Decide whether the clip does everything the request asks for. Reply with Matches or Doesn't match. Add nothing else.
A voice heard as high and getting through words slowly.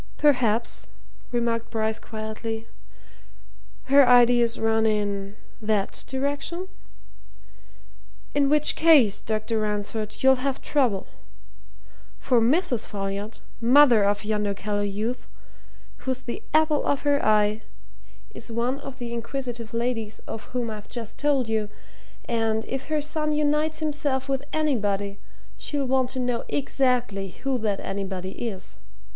Matches